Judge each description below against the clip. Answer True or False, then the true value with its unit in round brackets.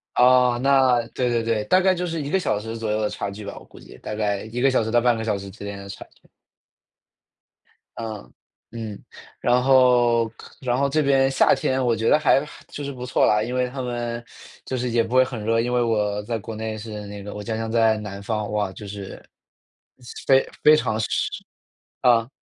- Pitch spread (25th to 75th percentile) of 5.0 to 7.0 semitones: False (3.0 semitones)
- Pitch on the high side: False (115 Hz)